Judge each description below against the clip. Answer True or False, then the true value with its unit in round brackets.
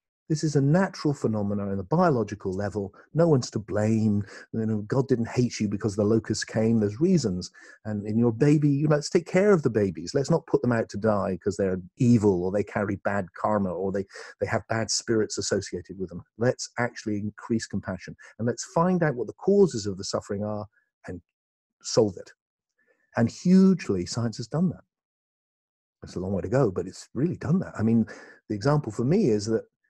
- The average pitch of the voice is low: True (110 Hz)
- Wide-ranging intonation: True (5.7 semitones)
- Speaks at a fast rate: True (210 wpm)